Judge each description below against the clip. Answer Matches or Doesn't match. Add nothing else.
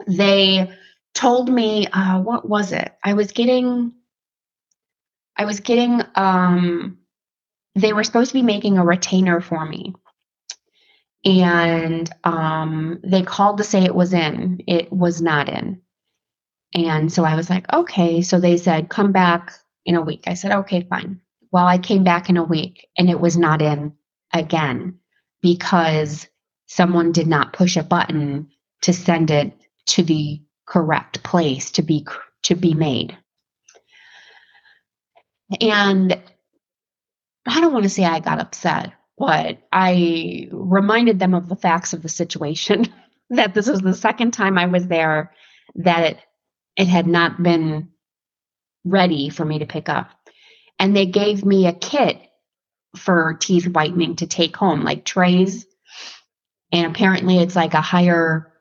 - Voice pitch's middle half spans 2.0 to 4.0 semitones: Matches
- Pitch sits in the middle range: Matches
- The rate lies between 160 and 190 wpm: Doesn't match